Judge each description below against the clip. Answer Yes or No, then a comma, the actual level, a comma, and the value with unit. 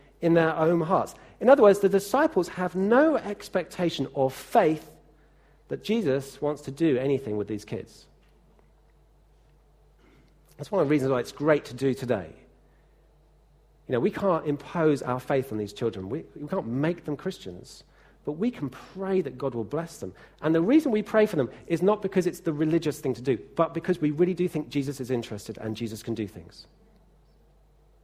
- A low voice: No, medium, 150 Hz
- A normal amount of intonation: No, wide, 5.7 semitones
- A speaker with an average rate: Yes, average, 190 wpm